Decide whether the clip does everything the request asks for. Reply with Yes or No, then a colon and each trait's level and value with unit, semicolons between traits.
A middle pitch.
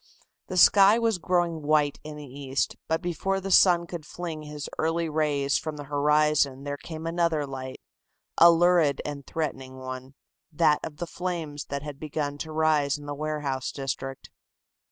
Yes: medium, 150 Hz